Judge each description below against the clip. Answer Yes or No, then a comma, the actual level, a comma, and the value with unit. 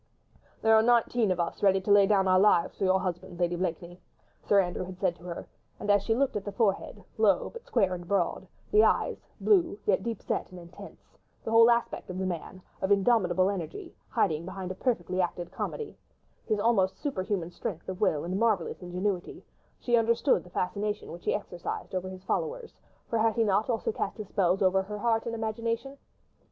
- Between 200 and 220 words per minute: Yes, fast, 205 wpm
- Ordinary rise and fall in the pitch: Yes, average, 3.6 semitones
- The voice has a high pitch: Yes, high, 195 Hz